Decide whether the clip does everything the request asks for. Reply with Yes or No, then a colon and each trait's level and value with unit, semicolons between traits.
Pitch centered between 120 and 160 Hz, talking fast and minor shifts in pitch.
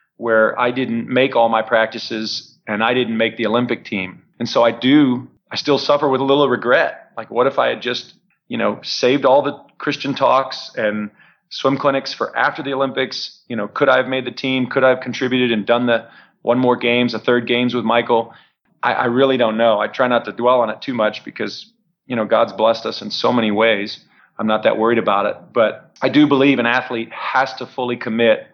Yes: low, 125 Hz; fast, 225 wpm; narrow, 2.3 semitones